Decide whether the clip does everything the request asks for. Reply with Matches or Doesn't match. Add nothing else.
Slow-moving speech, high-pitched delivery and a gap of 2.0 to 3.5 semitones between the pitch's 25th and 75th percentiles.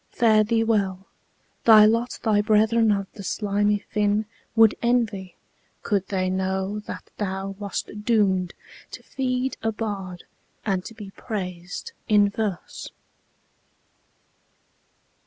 Matches